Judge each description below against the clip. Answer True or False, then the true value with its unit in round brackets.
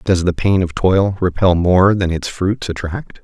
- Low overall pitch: True (90 Hz)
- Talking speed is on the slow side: False (205 wpm)